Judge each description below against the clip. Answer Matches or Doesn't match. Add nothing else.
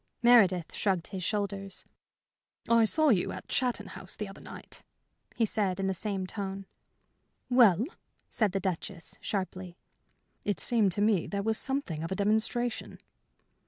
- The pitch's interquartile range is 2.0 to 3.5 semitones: Matches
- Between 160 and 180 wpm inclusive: Doesn't match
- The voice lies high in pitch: Matches